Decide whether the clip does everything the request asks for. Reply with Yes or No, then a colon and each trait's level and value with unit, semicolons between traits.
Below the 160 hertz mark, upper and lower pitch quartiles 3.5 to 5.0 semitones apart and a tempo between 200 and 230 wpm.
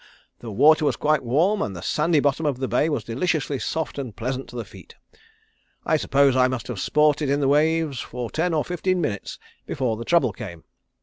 Yes: medium, 140 Hz; average, 4.2 semitones; fast, 205 wpm